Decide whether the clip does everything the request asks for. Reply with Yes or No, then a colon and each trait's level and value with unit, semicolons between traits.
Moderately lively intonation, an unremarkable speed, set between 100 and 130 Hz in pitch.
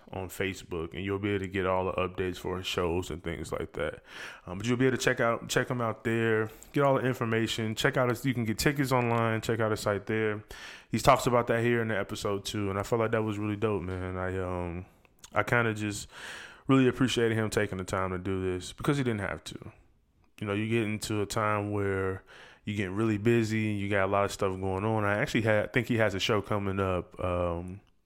No: average, 3.5 semitones; fast, 250 wpm; low, 105 Hz